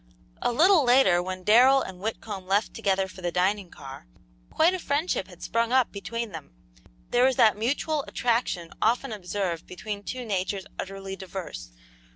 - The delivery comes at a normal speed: Yes, average, 165 wpm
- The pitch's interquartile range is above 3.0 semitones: Yes, average, 4.7 semitones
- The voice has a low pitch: No, high, 205 Hz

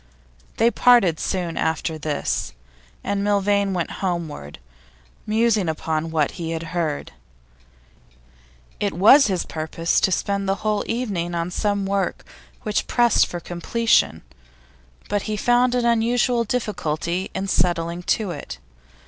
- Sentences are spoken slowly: Yes, slow, 130 wpm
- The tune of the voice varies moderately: Yes, average, 4.4 semitones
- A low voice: No, high, 190 Hz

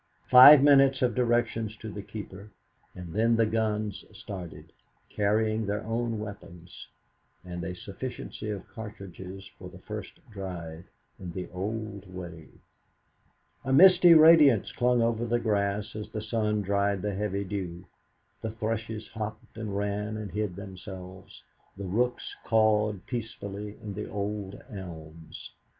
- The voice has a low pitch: Yes, low, 105 Hz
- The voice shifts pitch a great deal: No, average, 2.7 semitones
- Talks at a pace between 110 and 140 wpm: Yes, slow, 135 wpm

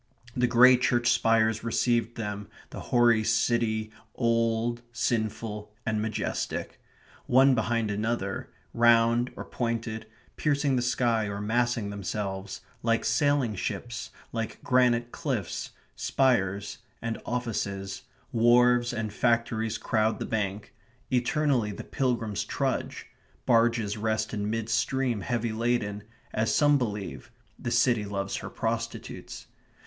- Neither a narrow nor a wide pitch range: No, narrow, 2.0 semitones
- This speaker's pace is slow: Yes, slow, 120 wpm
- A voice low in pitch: Yes, low, 115 Hz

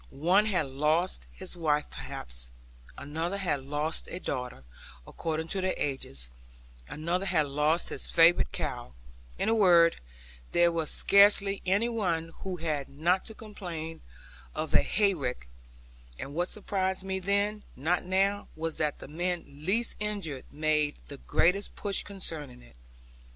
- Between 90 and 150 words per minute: Yes, average, 145 wpm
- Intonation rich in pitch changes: No, average, 4.4 semitones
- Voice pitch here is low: No, medium, 170 Hz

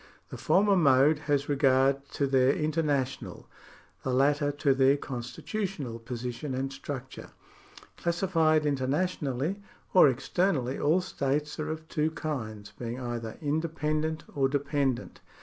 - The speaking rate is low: Yes, slow, 130 wpm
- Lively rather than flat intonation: No, average, 3.0 semitones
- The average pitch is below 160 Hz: Yes, medium, 140 Hz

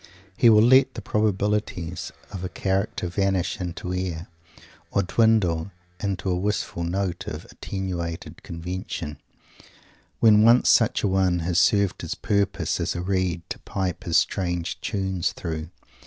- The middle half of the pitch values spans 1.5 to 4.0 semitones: Yes, narrow, 2.6 semitones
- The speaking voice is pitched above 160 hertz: No, very low, 95 Hz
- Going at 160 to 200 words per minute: No, average, 140 wpm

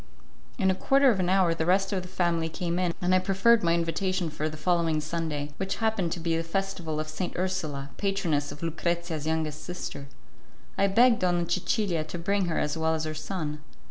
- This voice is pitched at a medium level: Yes, medium, 170 Hz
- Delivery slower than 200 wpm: No, fast, 205 wpm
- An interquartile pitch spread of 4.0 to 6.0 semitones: No, average, 3.1 semitones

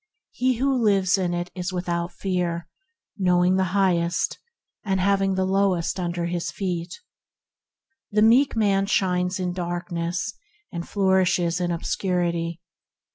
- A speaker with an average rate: No, slow, 130 wpm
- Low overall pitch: No, medium, 180 Hz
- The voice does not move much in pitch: Yes, narrow, 2.0 semitones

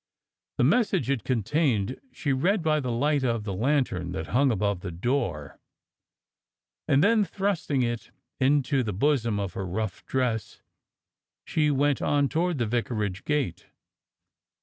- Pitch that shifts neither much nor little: No, wide, 5.8 semitones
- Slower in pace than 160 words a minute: Yes, average, 150 wpm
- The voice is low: Yes, low, 130 Hz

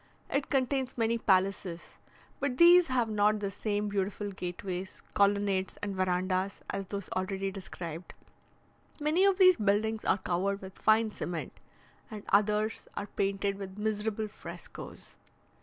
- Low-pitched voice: No, high, 205 Hz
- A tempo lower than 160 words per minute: Yes, slow, 135 wpm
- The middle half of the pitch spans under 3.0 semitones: Yes, narrow, 2.5 semitones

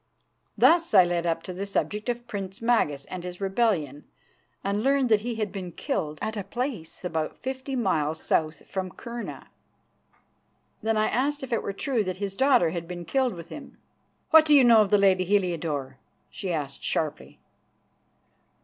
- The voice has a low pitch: No, high, 195 Hz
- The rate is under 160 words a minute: No, average, 175 wpm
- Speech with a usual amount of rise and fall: No, wide, 5.7 semitones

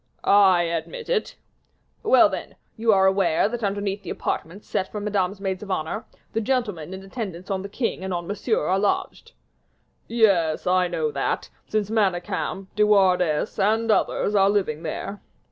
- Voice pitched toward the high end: Yes, high, 195 Hz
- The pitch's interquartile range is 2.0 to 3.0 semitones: Yes, average, 2.7 semitones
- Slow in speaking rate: No, average, 165 wpm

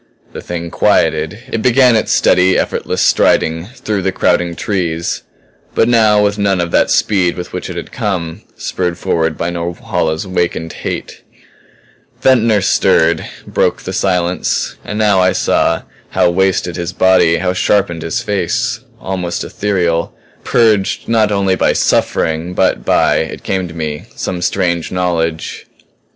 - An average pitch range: Yes, average, 3.2 semitones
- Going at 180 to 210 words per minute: No, average, 150 wpm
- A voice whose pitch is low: Yes, very low, 90 Hz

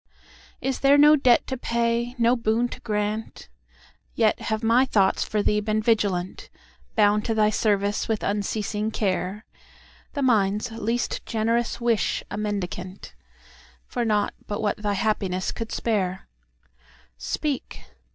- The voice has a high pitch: Yes, high, 215 Hz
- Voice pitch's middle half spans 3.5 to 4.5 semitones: No, narrow, 2.5 semitones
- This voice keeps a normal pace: No, slow, 120 wpm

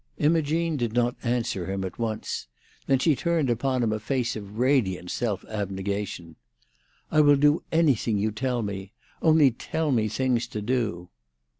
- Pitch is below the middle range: Yes, low, 120 Hz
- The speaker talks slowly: No, average, 160 wpm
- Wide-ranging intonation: No, average, 5.0 semitones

